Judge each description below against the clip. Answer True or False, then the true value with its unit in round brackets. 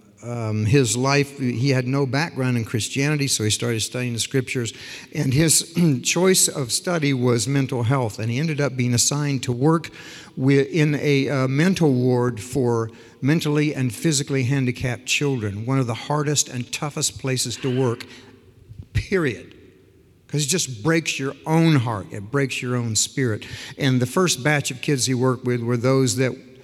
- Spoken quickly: False (175 wpm)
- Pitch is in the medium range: False (130 Hz)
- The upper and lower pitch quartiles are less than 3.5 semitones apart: True (3.0 semitones)